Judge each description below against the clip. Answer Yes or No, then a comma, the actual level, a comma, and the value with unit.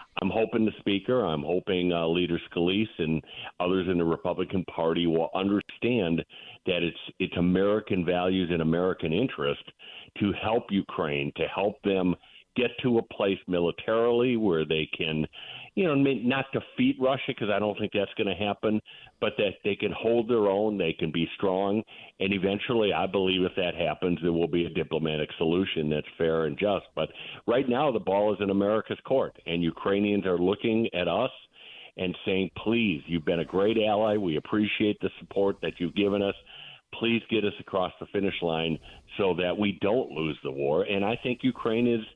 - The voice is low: Yes, very low, 95 Hz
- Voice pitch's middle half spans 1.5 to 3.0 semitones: No, average, 3.9 semitones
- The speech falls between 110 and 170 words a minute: No, average, 185 wpm